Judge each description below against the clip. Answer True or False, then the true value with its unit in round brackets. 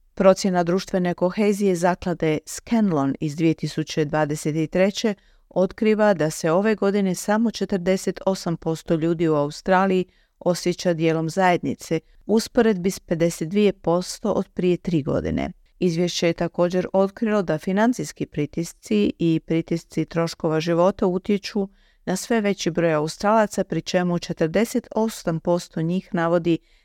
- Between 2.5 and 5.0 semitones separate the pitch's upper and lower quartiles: True (3.0 semitones)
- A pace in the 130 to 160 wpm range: False (120 wpm)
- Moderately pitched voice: True (180 Hz)